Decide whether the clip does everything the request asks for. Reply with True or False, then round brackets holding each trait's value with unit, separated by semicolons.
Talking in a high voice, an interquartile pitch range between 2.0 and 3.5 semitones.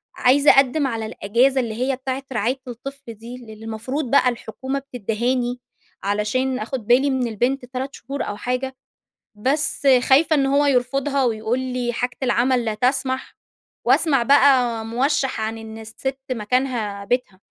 True (250 Hz; 3.0 semitones)